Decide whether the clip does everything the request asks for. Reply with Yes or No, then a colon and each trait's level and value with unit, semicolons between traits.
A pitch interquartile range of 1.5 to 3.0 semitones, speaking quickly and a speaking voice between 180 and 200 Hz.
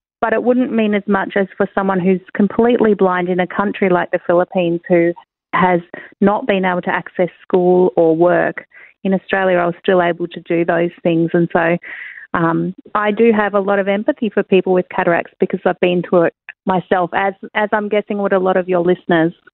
Yes: narrow, 2.4 semitones; fast, 210 wpm; medium, 185 Hz